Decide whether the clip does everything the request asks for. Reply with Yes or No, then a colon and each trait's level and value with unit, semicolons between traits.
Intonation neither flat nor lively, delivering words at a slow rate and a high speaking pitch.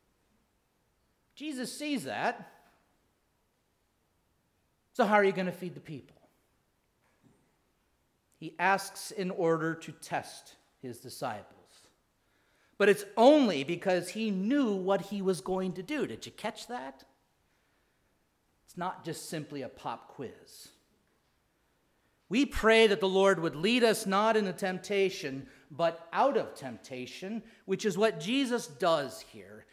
Yes: average, 4.2 semitones; slow, 130 wpm; high, 195 Hz